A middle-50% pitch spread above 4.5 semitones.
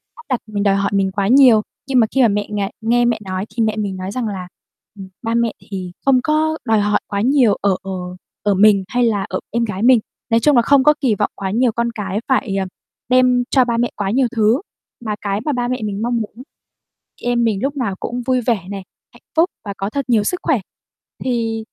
No: average, 3.8 semitones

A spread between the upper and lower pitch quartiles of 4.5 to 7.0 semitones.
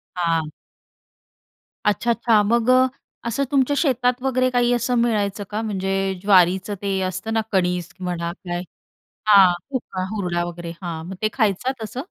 Yes: average, 5.0 semitones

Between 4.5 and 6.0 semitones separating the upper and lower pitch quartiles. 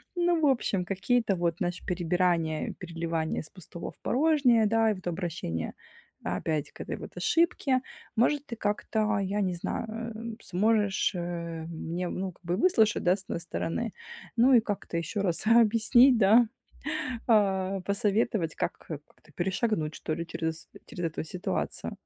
Yes: average, 5.0 semitones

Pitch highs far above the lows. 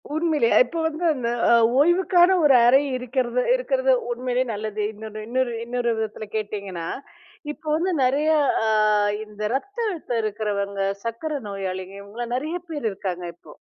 Yes: wide, 6.4 semitones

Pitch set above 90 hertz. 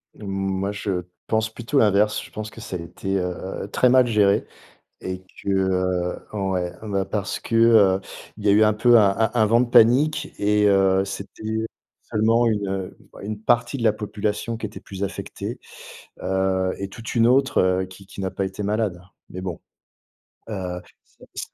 Yes: low, 100 Hz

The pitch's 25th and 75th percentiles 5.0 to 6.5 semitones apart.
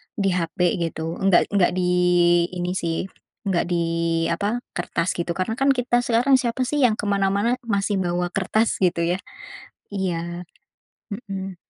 No: average, 3.9 semitones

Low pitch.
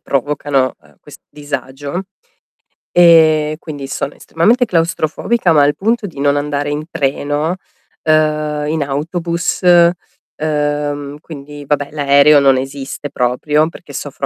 No: medium, 150 Hz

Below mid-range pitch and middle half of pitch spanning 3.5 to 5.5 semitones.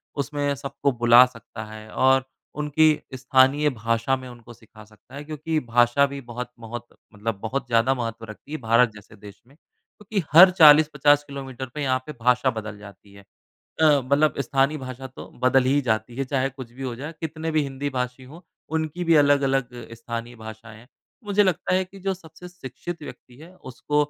Yes: low, 130 Hz; average, 3.9 semitones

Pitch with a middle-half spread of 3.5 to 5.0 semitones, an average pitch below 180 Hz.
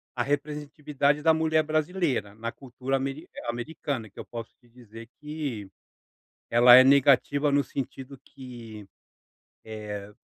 Yes: average, 4.1 semitones; low, 135 Hz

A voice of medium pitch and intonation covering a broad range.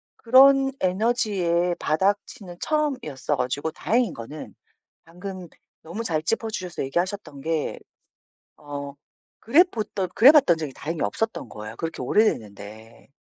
Yes: medium, 175 Hz; wide, 7.4 semitones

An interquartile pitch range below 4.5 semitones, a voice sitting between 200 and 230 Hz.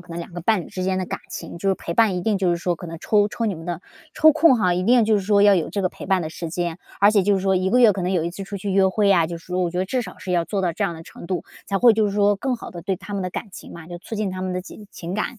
No: average, 2.8 semitones; high, 190 Hz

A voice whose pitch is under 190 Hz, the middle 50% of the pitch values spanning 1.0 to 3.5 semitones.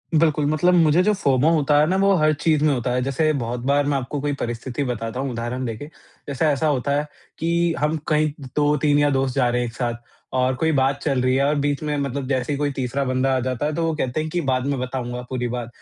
Yes: medium, 140 Hz; average, 3.1 semitones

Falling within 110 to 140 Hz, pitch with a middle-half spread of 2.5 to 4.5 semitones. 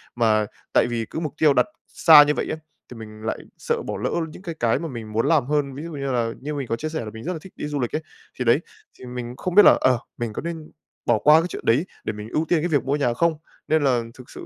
No: low, 135 Hz; average, 4.9 semitones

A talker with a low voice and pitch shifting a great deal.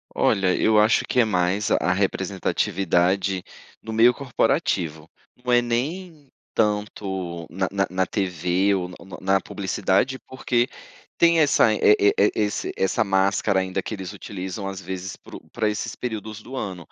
No: low, 100 Hz; average, 3.1 semitones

